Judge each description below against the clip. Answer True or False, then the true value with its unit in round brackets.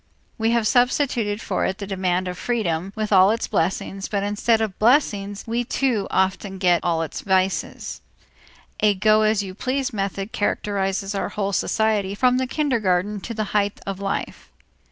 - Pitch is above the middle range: True (205 Hz)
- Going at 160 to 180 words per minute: True (175 wpm)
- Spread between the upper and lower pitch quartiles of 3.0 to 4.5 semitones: False (2.6 semitones)